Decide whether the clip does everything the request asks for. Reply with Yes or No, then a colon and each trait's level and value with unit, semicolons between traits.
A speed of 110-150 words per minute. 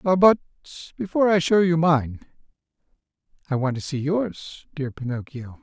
Yes: average, 140 wpm